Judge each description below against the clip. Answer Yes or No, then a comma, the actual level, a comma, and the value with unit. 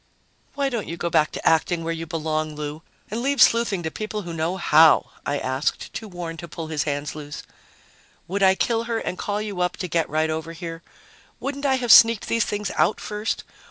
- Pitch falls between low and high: Yes, medium, 170 Hz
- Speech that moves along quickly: Yes, fast, 215 wpm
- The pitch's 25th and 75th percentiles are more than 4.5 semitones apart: Yes, average, 5.1 semitones